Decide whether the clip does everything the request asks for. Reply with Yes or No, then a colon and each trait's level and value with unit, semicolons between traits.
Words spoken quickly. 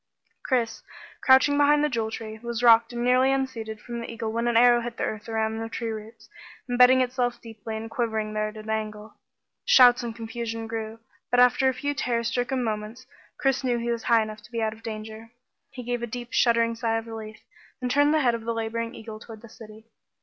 Yes: fast, 225 wpm